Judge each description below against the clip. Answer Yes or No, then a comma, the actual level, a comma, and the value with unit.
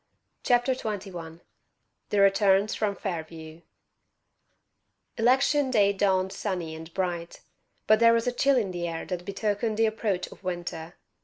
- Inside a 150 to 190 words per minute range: No, average, 140 wpm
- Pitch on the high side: Yes, high, 195 Hz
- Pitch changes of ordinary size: Yes, average, 4.2 semitones